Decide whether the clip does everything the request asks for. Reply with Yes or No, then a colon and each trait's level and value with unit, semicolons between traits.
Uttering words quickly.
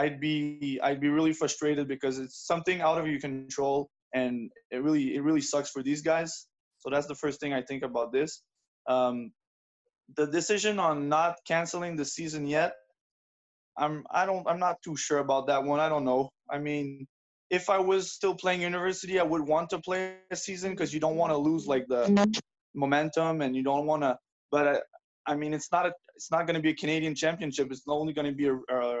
Yes: fast, 215 wpm